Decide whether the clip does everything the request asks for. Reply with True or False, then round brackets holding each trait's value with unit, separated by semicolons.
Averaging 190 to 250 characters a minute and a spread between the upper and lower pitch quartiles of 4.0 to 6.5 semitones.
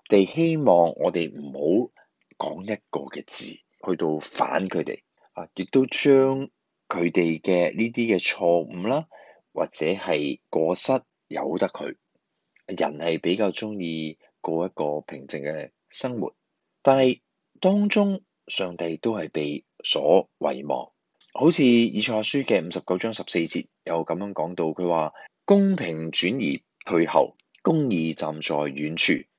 False (195 characters per minute; 8.2 semitones)